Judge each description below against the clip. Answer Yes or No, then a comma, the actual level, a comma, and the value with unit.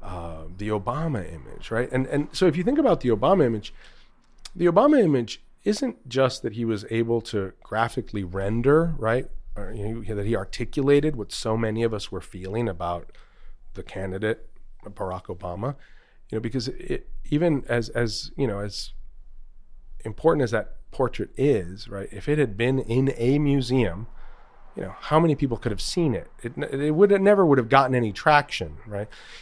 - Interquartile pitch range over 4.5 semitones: Yes, wide, 5.5 semitones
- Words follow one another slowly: No, average, 180 wpm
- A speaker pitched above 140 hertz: No, low, 120 Hz